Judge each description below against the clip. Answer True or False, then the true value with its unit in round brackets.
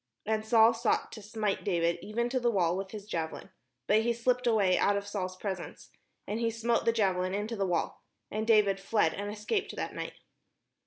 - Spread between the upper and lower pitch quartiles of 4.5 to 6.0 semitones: False (2.9 semitones)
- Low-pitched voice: False (210 Hz)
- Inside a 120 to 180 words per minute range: False (200 wpm)